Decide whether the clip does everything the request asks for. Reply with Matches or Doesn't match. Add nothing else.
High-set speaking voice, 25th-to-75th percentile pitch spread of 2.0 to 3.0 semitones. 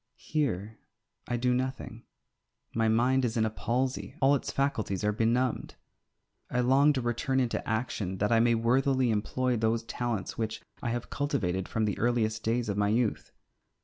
Doesn't match